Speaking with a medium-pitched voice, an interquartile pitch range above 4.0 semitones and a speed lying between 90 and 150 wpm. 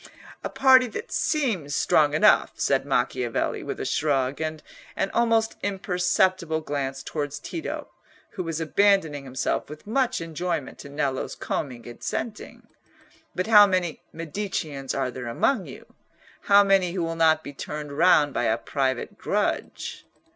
Yes: medium, 160 Hz; wide, 5.6 semitones; average, 145 wpm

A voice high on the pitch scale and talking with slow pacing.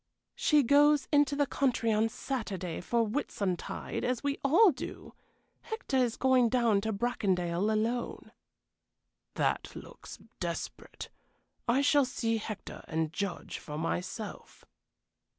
Yes: high, 235 Hz; slow, 120 wpm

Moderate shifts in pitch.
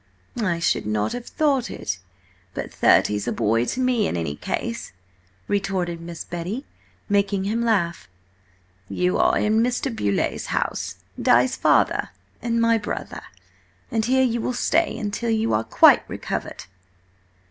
No: wide, 5.7 semitones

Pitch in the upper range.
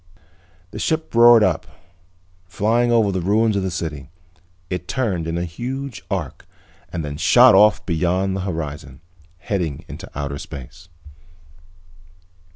No: very low, 90 Hz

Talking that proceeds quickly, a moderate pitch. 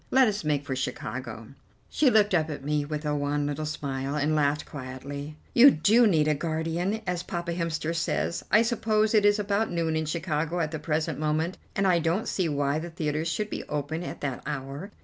Yes: fast, 210 wpm; medium, 160 Hz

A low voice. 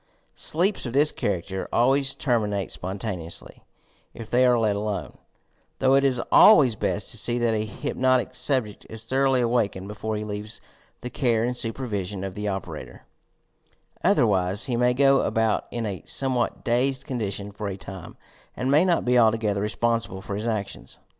Yes: low, 115 Hz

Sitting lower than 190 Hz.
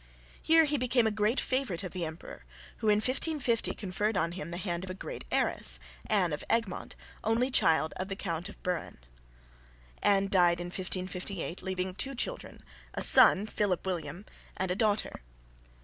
No: high, 195 Hz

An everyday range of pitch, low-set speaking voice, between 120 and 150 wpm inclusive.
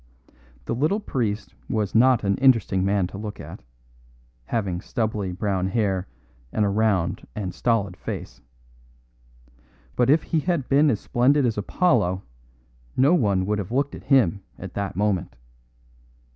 Yes: average, 4.9 semitones; low, 105 Hz; average, 145 wpm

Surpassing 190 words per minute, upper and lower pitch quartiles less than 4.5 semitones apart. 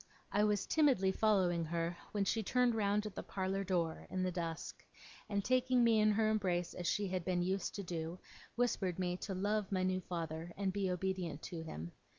Yes: average, 200 wpm; average, 3.1 semitones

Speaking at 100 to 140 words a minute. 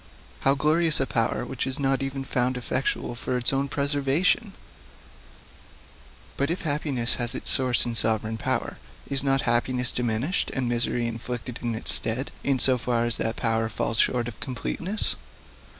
No: average, 165 wpm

